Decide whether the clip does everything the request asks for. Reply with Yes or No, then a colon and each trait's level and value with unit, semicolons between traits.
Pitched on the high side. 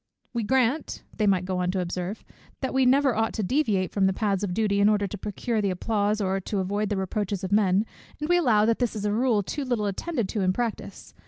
Yes: high, 210 Hz